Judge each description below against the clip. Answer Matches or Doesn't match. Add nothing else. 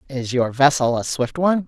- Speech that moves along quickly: Matches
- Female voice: Matches